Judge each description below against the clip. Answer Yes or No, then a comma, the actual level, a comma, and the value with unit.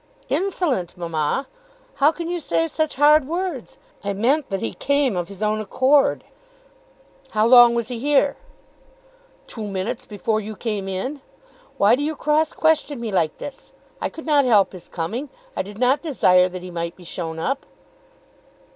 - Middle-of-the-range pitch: No, high, 235 Hz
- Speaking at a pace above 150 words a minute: Yes, average, 170 wpm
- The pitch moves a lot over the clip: Yes, wide, 7.1 semitones